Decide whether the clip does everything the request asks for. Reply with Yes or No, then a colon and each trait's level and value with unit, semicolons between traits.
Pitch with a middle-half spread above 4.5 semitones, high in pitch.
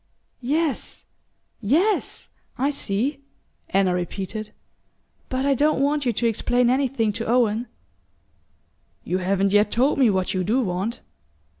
Yes: wide, 5.4 semitones; high, 230 Hz